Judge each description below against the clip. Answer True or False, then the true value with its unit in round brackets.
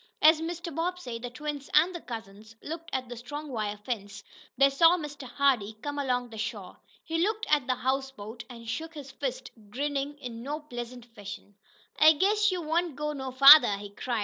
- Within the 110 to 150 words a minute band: False (190 wpm)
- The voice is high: True (270 Hz)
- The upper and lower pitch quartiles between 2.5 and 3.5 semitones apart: False (4.6 semitones)